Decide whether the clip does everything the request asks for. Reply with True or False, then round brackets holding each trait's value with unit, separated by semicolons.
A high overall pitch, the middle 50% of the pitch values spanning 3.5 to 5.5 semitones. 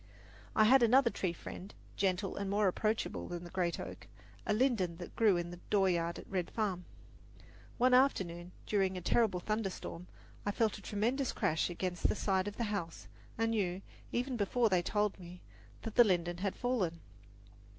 True (195 Hz; 3.9 semitones)